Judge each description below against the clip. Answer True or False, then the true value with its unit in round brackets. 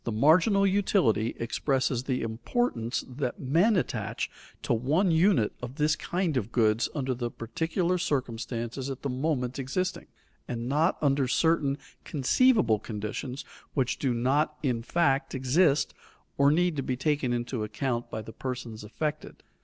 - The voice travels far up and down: False (4.8 semitones)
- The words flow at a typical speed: True (145 wpm)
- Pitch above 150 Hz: False (135 Hz)